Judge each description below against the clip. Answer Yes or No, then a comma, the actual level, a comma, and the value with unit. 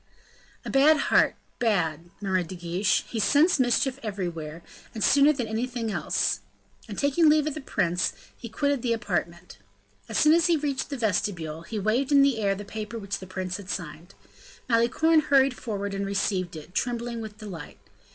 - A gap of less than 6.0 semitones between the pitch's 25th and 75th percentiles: No, wide, 6.3 semitones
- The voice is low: No, high, 215 Hz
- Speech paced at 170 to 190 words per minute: Yes, average, 180 wpm